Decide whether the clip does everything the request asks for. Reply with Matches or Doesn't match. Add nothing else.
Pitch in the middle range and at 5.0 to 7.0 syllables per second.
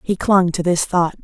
Doesn't match